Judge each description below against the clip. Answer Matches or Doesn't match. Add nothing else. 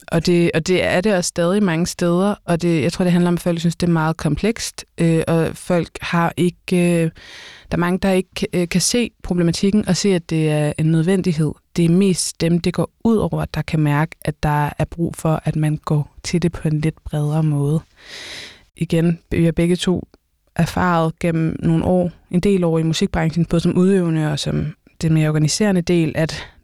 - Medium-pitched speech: Matches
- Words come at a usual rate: Matches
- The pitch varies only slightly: Matches